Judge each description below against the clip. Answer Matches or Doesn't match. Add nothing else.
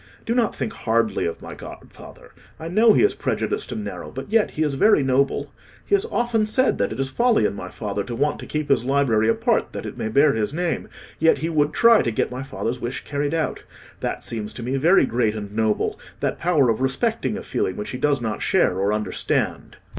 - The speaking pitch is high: Doesn't match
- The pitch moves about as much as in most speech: Doesn't match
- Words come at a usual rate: Doesn't match